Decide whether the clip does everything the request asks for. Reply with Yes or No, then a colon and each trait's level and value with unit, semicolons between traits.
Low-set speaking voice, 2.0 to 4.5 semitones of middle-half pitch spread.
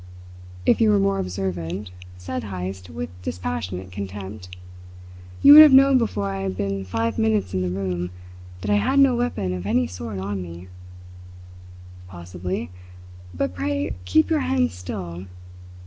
Yes: very low, 95 Hz; average, 3.4 semitones